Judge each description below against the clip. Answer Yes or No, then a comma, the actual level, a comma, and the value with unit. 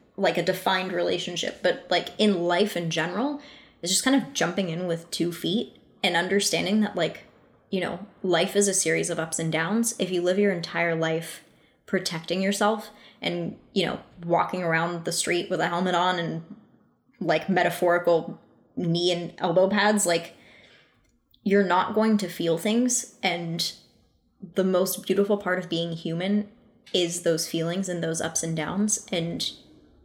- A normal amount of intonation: Yes, average, 3.1 semitones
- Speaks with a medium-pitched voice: Yes, medium, 180 Hz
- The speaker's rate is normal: Yes, average, 165 wpm